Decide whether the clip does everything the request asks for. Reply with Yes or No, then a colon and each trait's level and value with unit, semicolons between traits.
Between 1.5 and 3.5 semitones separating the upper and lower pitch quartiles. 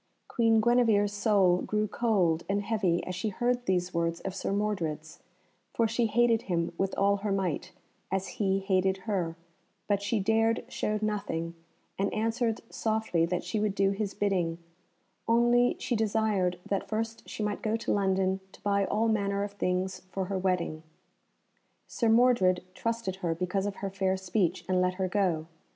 Yes: average, 3.0 semitones